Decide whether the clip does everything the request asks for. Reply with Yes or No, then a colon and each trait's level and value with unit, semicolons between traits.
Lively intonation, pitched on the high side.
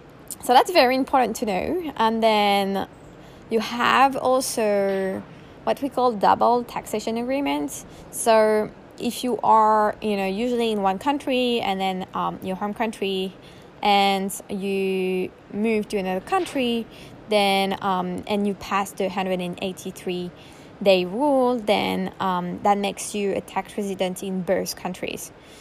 No: average, 3.6 semitones; high, 205 Hz